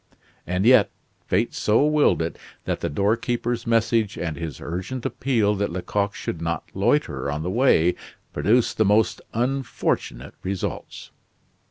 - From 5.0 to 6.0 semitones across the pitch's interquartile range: Yes, wide, 5.4 semitones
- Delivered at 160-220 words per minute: No, average, 140 wpm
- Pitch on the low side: Yes, low, 105 Hz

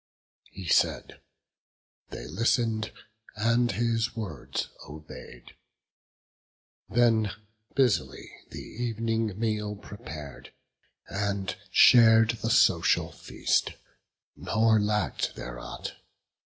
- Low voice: Yes, low, 110 Hz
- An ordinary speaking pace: No, slow, 85 wpm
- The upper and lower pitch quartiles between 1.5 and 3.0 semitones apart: Yes, narrow, 2.5 semitones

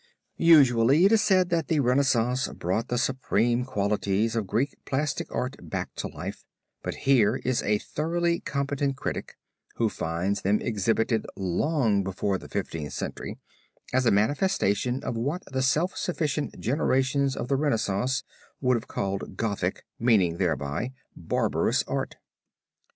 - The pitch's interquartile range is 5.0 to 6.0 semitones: Yes, wide, 5.5 semitones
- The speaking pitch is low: Yes, low, 125 Hz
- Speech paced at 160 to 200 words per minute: No, average, 140 wpm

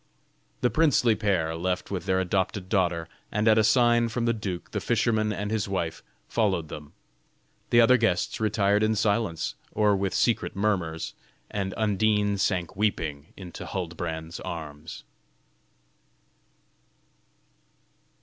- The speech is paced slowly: Yes, slow, 130 wpm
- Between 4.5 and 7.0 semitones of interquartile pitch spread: No, average, 3.8 semitones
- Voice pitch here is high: No, low, 100 Hz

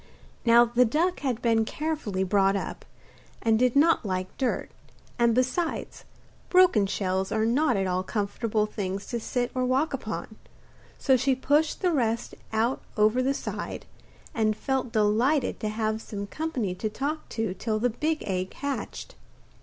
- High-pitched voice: Yes, high, 230 Hz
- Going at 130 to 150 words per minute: No, average, 160 wpm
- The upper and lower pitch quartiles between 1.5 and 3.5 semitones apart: No, average, 4.1 semitones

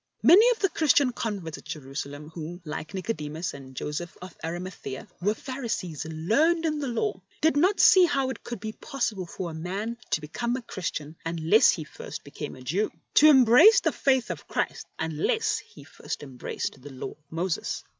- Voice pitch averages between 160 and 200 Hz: Yes, medium, 185 Hz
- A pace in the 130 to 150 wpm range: No, fast, 205 wpm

